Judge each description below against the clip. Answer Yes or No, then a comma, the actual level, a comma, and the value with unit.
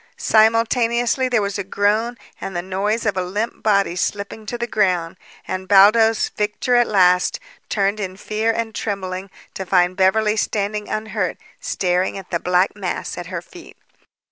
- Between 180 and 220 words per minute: No, average, 165 wpm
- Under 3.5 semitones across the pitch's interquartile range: Yes, average, 2.9 semitones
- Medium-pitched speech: No, high, 205 Hz